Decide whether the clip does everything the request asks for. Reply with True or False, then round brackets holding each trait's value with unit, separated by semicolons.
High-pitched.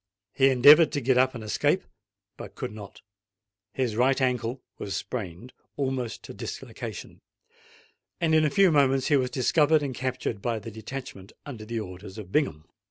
False (125 Hz)